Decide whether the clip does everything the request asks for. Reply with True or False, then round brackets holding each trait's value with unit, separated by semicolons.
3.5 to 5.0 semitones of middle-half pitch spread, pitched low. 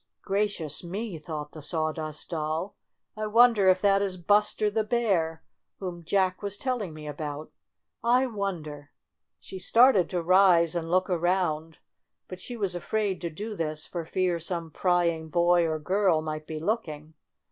False (4.0 semitones; 175 Hz)